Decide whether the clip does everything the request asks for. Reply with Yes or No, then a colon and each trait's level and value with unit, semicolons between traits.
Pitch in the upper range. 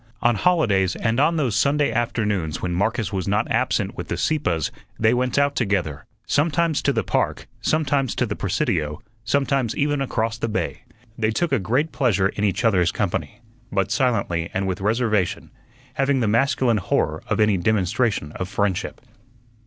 No: low, 110 Hz